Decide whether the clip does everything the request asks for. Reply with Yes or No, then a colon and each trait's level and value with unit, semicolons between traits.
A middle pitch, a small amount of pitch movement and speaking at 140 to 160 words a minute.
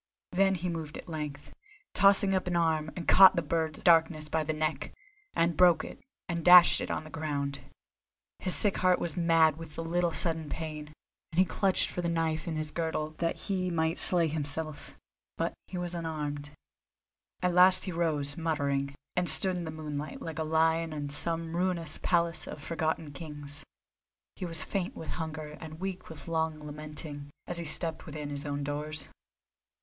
No: medium, 160 Hz; narrow, 2.1 semitones; average, 185 wpm